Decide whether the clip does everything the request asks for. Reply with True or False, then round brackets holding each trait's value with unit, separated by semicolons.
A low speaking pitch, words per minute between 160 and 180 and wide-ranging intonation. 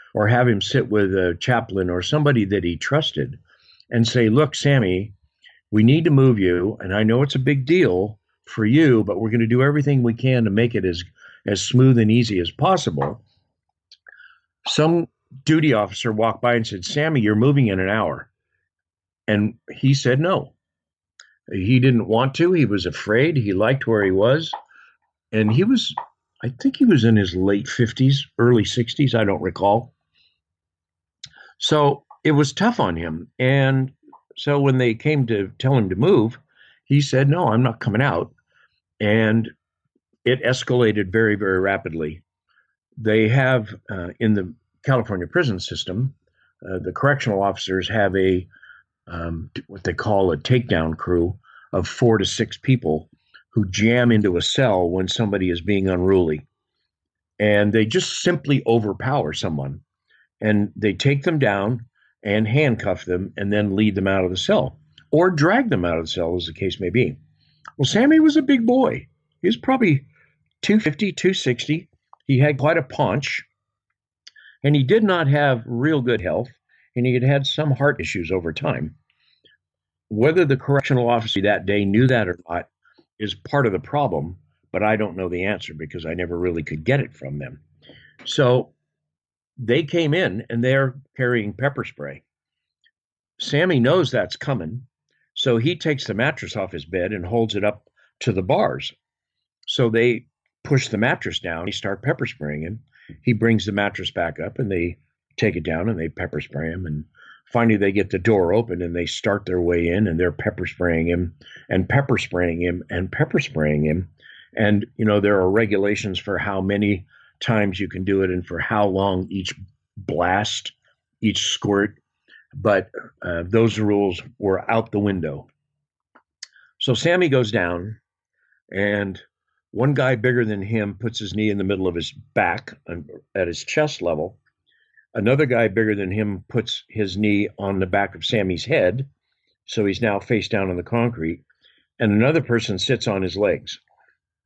True (110 Hz; 175 wpm; 5.7 semitones)